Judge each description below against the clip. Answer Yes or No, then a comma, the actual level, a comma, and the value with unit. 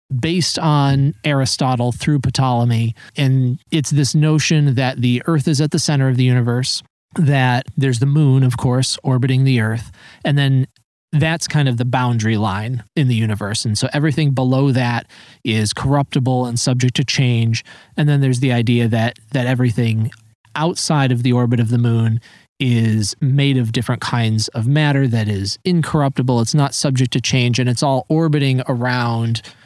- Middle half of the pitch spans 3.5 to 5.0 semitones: No, average, 2.9 semitones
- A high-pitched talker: No, low, 130 Hz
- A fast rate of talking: No, average, 170 wpm